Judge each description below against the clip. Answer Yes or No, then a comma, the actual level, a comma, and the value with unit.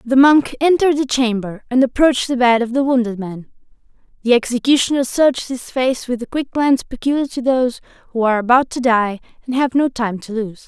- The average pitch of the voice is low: No, very high, 250 Hz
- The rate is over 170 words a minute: Yes, average, 200 wpm